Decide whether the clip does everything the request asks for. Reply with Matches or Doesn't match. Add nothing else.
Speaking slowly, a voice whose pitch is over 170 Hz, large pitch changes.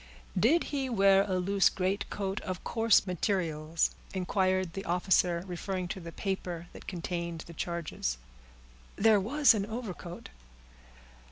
Doesn't match